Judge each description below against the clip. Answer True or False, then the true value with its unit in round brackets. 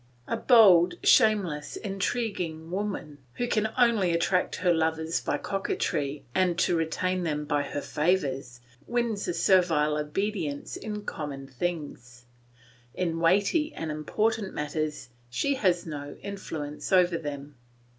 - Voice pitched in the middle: True (170 Hz)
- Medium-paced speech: False (125 wpm)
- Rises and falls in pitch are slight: False (4.9 semitones)